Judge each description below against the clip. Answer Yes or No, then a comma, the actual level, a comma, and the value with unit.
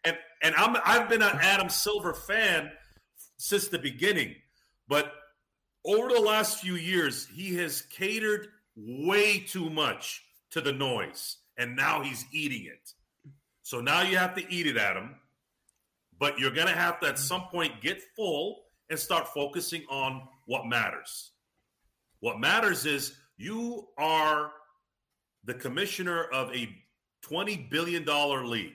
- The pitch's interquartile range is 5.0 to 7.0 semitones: Yes, average, 5.3 semitones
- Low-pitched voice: No, medium, 160 Hz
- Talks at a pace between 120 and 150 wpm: Yes, average, 145 wpm